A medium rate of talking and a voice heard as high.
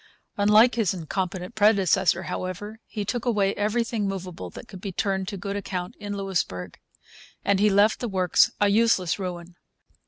Yes: average, 160 wpm; high, 200 Hz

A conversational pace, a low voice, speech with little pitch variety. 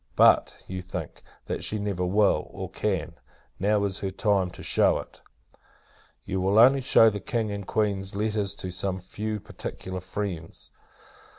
Yes: average, 160 wpm; low, 100 Hz; narrow, 2.3 semitones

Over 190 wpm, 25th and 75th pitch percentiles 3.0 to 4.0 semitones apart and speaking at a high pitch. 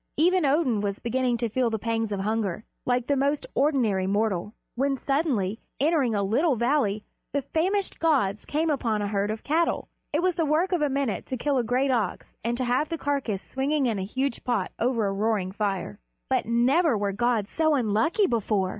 No: average, 200 wpm; average, 5.3 semitones; high, 245 Hz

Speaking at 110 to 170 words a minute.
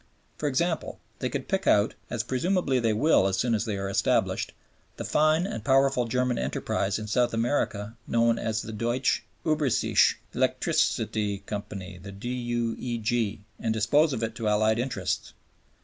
Yes: average, 150 wpm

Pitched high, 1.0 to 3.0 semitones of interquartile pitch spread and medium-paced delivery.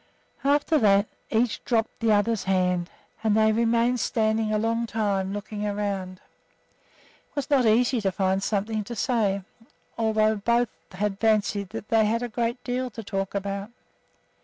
Yes: high, 215 Hz; narrow, 2.6 semitones; average, 160 wpm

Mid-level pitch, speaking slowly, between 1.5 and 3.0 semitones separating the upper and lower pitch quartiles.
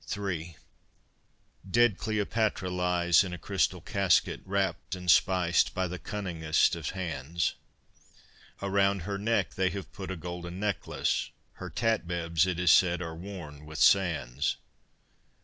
No: very low, 90 Hz; slow, 130 wpm; narrow, 2.6 semitones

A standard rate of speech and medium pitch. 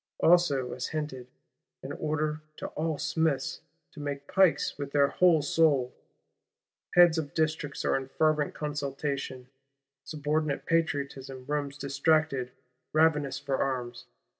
No: slow, 120 wpm; medium, 145 Hz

